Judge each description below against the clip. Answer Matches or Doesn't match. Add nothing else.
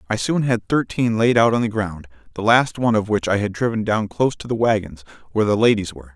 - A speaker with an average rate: Doesn't match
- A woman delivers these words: Doesn't match